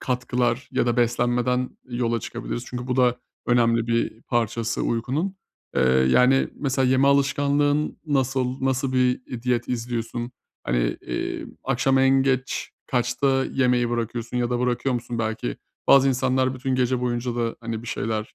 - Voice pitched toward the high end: No, low, 125 Hz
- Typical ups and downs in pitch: No, narrow, 1.9 semitones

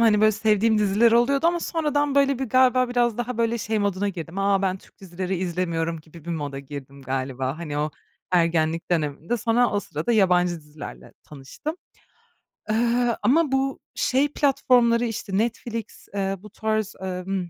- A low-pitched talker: No, high, 205 Hz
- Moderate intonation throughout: No, wide, 6.0 semitones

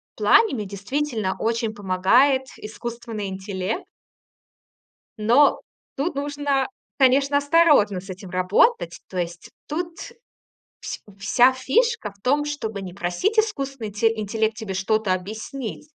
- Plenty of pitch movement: Yes, wide, 6.2 semitones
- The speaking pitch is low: No, high, 225 Hz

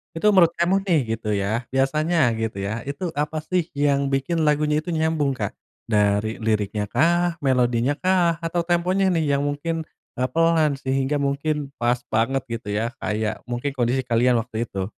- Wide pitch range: Yes, wide, 6.0 semitones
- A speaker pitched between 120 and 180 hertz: Yes, medium, 140 Hz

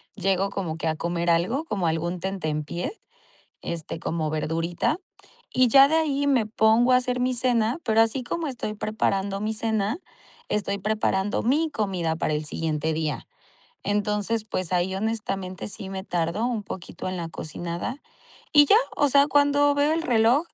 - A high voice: Yes, high, 205 Hz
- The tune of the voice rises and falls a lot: Yes, wide, 6.4 semitones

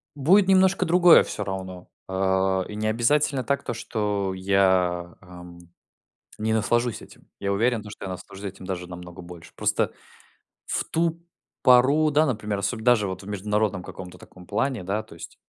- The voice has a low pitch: Yes, low, 105 Hz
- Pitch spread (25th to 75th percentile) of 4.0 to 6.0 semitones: Yes, average, 4.7 semitones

